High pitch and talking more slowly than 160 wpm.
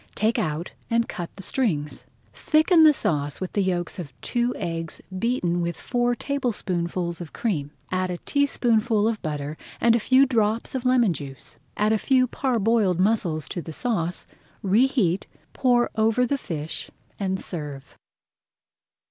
Yes: high, 205 Hz; average, 150 wpm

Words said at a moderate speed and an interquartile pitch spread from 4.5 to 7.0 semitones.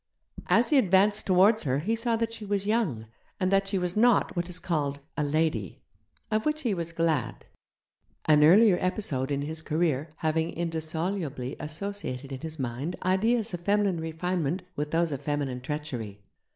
Yes: average, 170 wpm; average, 5.2 semitones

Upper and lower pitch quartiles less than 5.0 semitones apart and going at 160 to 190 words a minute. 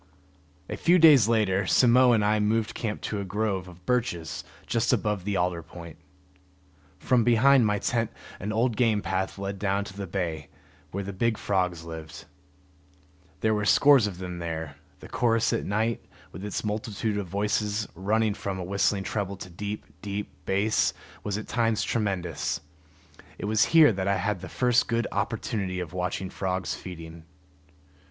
Yes: average, 3.3 semitones; average, 170 wpm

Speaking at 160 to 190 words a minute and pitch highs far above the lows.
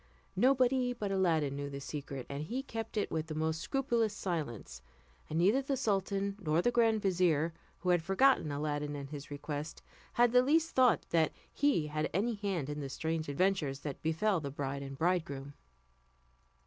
Yes: average, 175 wpm; wide, 6.8 semitones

